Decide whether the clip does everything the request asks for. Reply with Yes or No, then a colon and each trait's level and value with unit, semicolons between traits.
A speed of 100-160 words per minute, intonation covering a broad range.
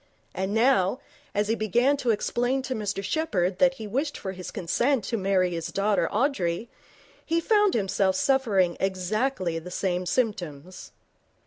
Yes: average, 150 wpm; wide, 5.7 semitones